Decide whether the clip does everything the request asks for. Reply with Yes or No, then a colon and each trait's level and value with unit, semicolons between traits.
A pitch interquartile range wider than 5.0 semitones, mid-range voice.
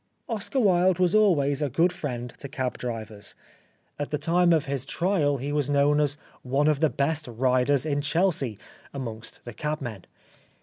No: average, 4.3 semitones; medium, 145 Hz